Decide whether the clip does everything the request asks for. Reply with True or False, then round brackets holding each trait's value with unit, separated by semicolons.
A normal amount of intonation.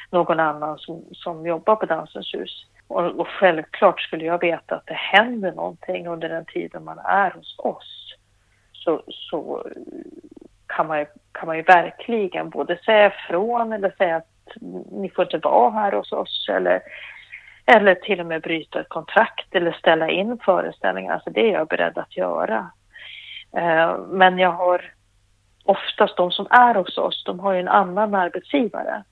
True (3.5 semitones)